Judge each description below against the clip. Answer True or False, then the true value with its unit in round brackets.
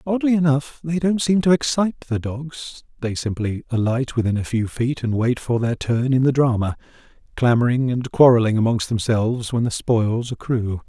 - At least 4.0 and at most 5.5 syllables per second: True (5.0 syllables/s)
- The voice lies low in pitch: True (125 Hz)